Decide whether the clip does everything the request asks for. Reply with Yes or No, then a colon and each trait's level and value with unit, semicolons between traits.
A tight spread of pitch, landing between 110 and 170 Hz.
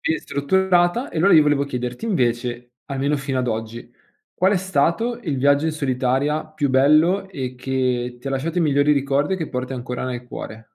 No: average, 4.1 semitones; medium, 140 Hz